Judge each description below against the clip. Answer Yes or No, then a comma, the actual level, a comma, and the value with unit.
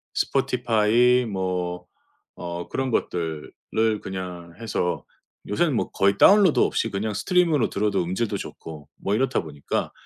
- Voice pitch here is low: Yes, low, 100 Hz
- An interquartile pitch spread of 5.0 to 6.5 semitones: Yes, wide, 5.6 semitones